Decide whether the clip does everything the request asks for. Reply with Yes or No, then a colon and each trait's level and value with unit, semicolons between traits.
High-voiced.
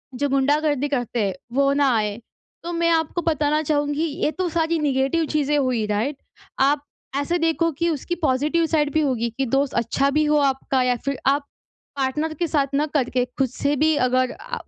Yes: very high, 285 Hz